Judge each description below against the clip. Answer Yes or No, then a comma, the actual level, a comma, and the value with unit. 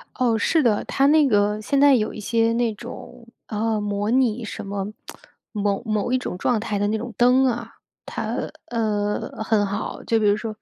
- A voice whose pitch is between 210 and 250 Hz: Yes, high, 220 Hz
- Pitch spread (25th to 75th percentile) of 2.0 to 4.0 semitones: Yes, narrow, 2.6 semitones